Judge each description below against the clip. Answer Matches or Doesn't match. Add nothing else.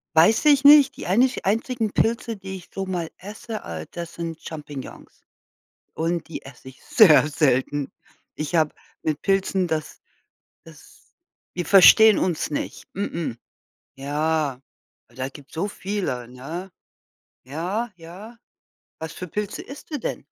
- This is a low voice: Doesn't match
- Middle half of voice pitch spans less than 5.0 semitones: Doesn't match